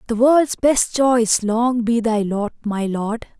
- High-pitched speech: Yes, high, 230 Hz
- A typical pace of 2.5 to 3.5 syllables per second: Yes, 3.3 syllables/s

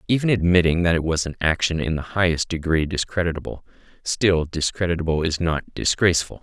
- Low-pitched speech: Yes, very low, 85 Hz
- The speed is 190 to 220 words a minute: No, average, 160 wpm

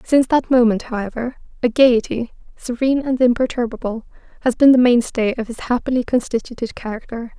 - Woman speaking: Yes, female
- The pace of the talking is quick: No, average, 145 wpm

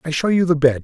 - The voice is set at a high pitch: No, medium, 155 Hz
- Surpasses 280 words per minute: Yes, fast, 360 wpm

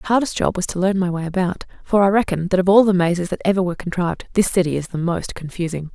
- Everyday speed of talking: No, fast, 270 wpm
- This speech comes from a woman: Yes, female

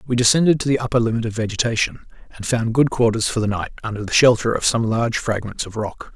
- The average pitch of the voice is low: Yes, low, 115 Hz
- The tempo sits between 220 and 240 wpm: Yes, fast, 235 wpm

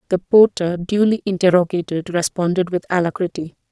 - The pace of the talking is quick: No, slow, 115 wpm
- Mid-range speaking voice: Yes, medium, 180 Hz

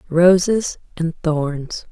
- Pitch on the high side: No, medium, 170 Hz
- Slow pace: Yes, slow, 95 wpm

